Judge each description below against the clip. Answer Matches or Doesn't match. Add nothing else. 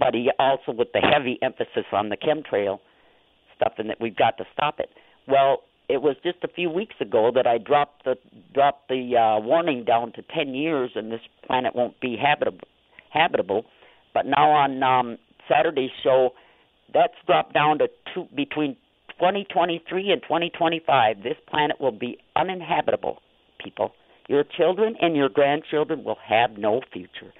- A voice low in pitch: Doesn't match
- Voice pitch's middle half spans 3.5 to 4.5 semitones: Doesn't match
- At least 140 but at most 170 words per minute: Matches